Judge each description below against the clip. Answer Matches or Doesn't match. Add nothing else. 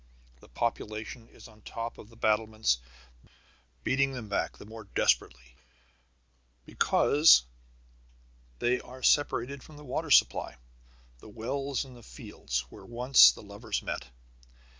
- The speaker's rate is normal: Doesn't match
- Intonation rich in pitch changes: Doesn't match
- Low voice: Matches